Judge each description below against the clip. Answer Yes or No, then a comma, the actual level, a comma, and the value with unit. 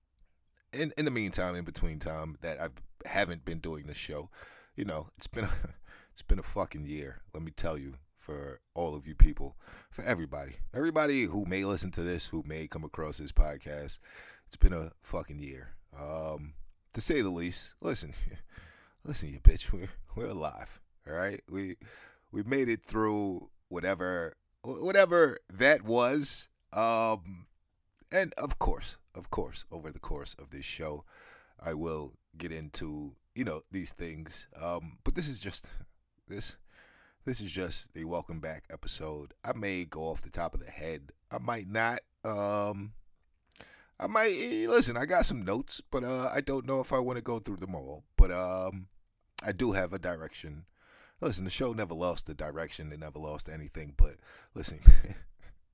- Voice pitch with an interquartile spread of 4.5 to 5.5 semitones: Yes, average, 4.9 semitones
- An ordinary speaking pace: Yes, average, 175 wpm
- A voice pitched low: Yes, very low, 85 Hz